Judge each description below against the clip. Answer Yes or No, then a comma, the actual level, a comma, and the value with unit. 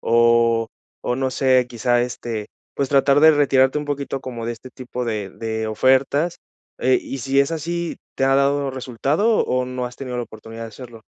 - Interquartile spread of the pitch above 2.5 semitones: Yes, average, 2.9 semitones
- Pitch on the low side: Yes, low, 130 Hz